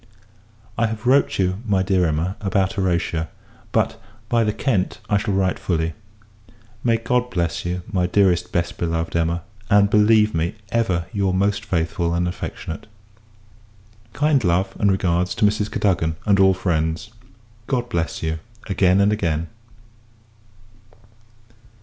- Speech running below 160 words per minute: Yes, average, 140 wpm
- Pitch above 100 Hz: No, very low, 95 Hz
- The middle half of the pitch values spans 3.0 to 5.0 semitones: Yes, average, 3.7 semitones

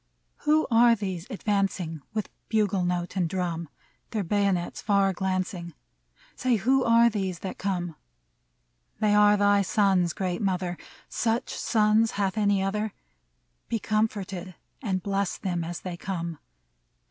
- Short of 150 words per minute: Yes, slow, 135 wpm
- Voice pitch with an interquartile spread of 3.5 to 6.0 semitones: No, average, 2.9 semitones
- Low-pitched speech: No, high, 195 Hz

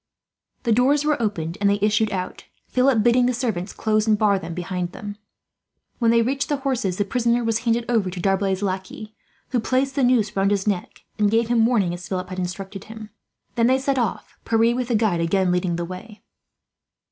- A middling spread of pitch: Yes, average, 3.9 semitones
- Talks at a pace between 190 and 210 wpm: Yes, fast, 205 wpm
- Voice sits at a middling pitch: No, high, 215 Hz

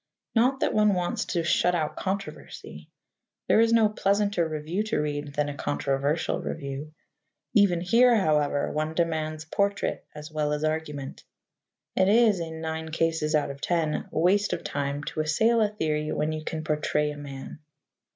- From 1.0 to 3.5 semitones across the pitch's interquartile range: No, average, 4.7 semitones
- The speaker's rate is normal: Yes, average, 165 wpm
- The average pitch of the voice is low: No, medium, 160 Hz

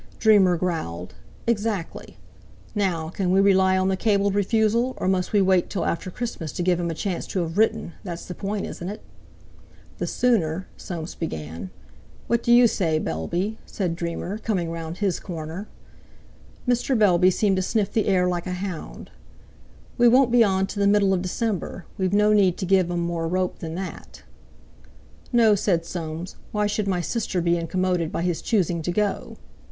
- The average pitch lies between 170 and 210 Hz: Yes, medium, 185 Hz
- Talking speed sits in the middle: Yes, average, 180 wpm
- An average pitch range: Yes, average, 3.2 semitones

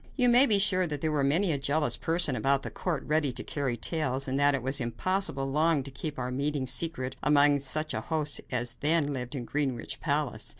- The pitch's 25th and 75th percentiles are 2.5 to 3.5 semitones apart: Yes, average, 3.0 semitones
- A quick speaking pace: Yes, fast, 215 wpm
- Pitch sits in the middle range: Yes, medium, 145 Hz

